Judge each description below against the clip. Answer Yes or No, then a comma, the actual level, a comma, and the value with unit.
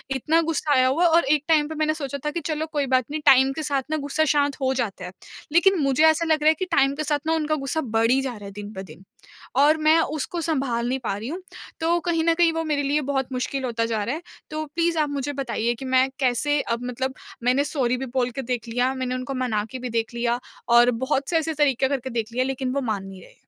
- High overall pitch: Yes, very high, 270 Hz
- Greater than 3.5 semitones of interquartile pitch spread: Yes, average, 3.9 semitones